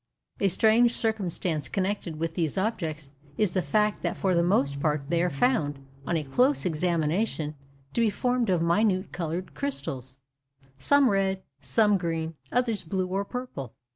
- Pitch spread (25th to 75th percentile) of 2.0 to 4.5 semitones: No, wide, 5.5 semitones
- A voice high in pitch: No, medium, 180 Hz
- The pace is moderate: Yes, average, 155 wpm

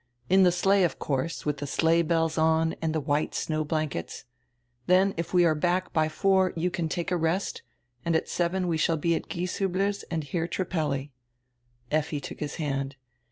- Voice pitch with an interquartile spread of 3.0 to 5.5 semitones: No, narrow, 2.5 semitones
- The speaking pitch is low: No, medium, 165 Hz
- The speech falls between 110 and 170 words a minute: No, average, 190 wpm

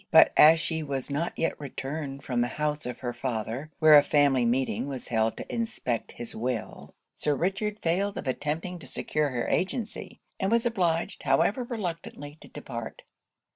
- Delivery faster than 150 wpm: Yes, average, 175 wpm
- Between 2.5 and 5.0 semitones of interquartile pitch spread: No, wide, 5.4 semitones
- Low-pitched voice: No, medium, 150 Hz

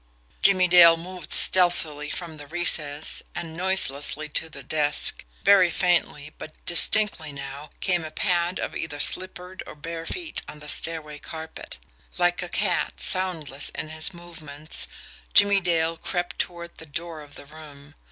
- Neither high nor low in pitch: Yes, medium, 165 Hz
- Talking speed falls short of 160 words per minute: Yes, average, 150 wpm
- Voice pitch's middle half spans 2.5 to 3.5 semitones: Yes, average, 2.9 semitones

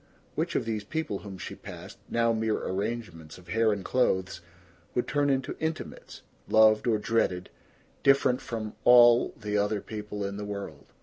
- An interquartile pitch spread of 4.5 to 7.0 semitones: No, average, 2.9 semitones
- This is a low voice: Yes, low, 110 Hz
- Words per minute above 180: No, average, 165 wpm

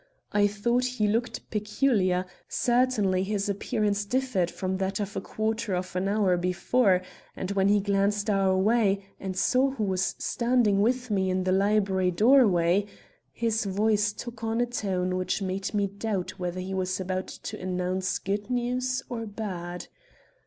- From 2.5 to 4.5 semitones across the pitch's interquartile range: Yes, average, 3.1 semitones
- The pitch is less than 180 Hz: No, high, 200 Hz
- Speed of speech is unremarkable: Yes, average, 160 wpm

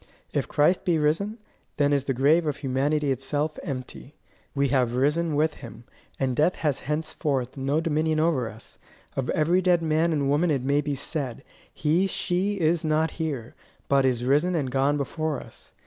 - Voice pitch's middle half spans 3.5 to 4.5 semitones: No, average, 2.9 semitones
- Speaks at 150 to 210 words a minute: Yes, average, 180 wpm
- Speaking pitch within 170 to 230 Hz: No, medium, 150 Hz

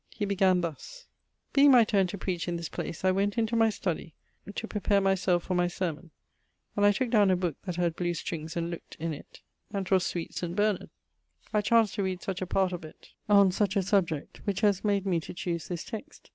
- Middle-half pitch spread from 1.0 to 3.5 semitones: Yes, average, 2.8 semitones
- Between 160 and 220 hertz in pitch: Yes, high, 190 Hz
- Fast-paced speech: Yes, fast, 230 wpm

